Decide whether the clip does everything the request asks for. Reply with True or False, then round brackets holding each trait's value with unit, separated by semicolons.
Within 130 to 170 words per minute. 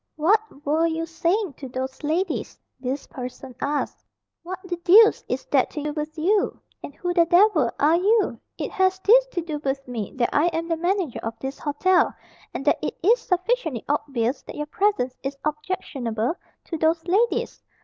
False (180 wpm)